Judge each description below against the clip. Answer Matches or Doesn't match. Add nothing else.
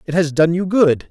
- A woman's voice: Doesn't match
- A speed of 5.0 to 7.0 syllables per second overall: Matches